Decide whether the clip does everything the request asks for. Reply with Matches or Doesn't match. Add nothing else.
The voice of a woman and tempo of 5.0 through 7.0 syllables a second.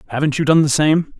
Doesn't match